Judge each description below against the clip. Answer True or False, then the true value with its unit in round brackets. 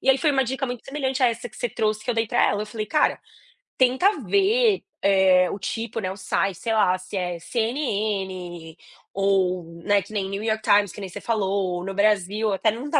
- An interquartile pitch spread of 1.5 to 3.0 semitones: False (4.3 semitones)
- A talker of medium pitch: False (210 Hz)